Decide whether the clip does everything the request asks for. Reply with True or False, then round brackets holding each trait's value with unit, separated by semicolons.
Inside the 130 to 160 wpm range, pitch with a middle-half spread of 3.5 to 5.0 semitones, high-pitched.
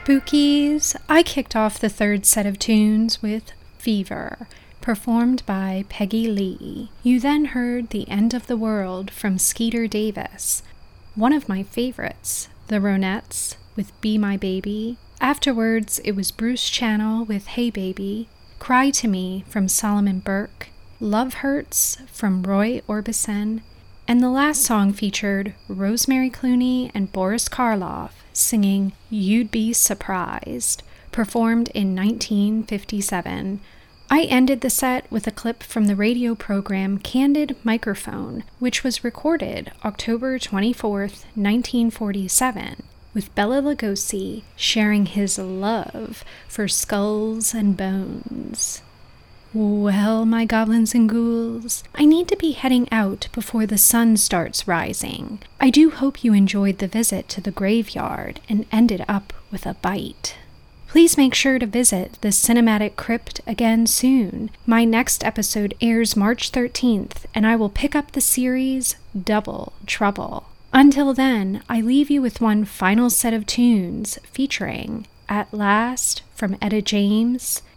False (135 wpm; 3.1 semitones; 225 Hz)